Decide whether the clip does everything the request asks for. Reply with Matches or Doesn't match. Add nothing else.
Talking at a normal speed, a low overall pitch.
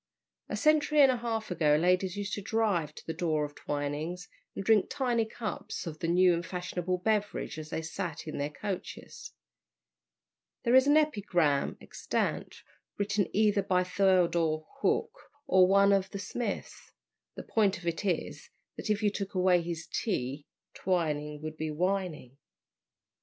Doesn't match